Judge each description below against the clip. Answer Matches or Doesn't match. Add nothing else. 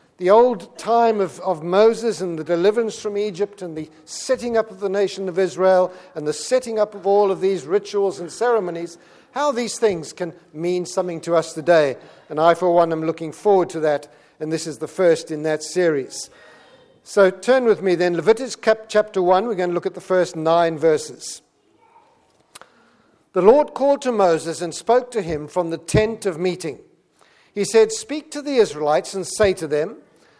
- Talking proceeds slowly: Doesn't match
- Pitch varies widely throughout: Doesn't match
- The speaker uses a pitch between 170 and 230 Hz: Matches